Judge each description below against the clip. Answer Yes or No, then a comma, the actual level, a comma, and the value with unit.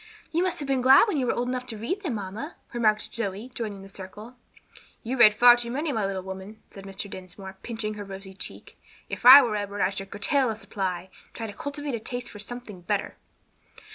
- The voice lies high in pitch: Yes, high, 215 Hz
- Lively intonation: No, average, 4.1 semitones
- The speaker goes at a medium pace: No, fast, 225 wpm